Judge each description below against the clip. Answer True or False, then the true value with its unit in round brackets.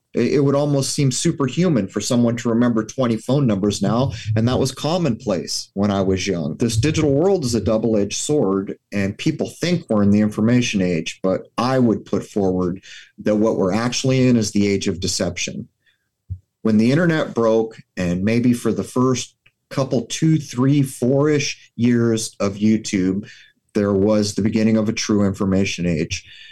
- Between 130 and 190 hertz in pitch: False (110 Hz)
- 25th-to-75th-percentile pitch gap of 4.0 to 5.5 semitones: True (4.5 semitones)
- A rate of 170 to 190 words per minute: True (175 wpm)